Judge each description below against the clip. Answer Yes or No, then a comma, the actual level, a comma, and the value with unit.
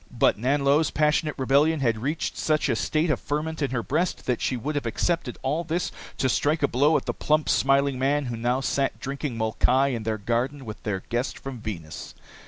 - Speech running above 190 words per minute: Yes, fast, 205 wpm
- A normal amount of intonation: Yes, average, 3.9 semitones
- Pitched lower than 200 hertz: Yes, low, 135 Hz